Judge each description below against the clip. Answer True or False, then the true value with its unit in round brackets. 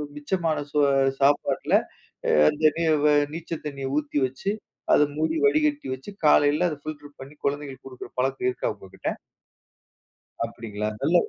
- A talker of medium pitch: True (145 Hz)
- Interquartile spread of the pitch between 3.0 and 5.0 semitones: False (2.4 semitones)